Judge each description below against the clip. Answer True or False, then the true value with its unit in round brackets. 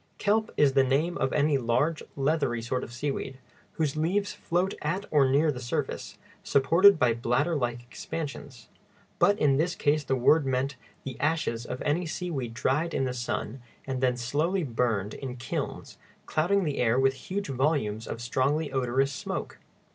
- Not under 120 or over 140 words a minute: False (170 wpm)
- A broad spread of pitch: False (4.0 semitones)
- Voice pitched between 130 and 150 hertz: True (135 Hz)